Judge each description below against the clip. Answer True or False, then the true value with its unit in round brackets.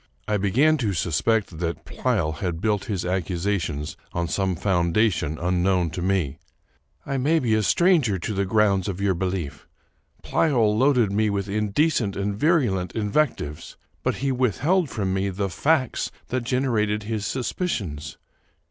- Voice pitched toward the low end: True (100 Hz)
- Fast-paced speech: False (155 wpm)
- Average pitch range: True (4.9 semitones)